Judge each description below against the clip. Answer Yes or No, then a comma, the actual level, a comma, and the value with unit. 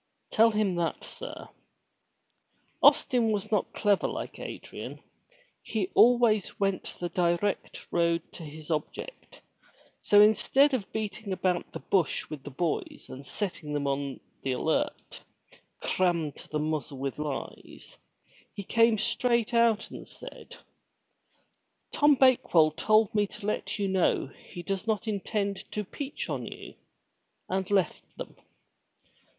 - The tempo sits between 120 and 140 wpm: Yes, slow, 135 wpm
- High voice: Yes, high, 195 Hz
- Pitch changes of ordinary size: Yes, average, 4.6 semitones